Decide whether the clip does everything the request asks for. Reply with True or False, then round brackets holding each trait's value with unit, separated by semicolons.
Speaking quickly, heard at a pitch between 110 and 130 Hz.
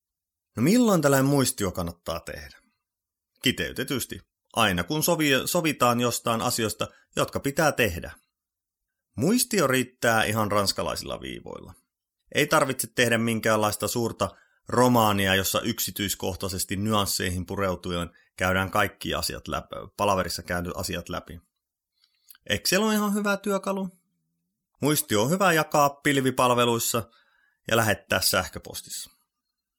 False (105 wpm; 115 Hz)